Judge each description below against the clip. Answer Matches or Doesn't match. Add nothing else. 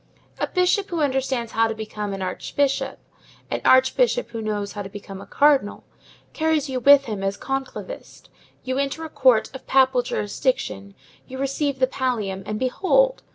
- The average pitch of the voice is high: Matches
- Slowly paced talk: Doesn't match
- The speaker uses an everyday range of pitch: Matches